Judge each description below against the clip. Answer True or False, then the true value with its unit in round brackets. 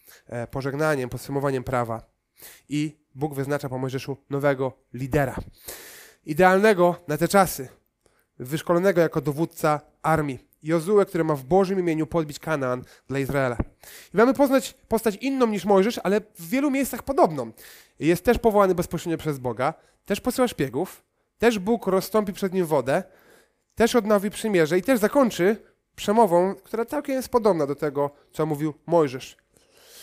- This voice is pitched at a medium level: True (165 Hz)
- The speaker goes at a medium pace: True (140 wpm)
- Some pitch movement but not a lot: False (7.0 semitones)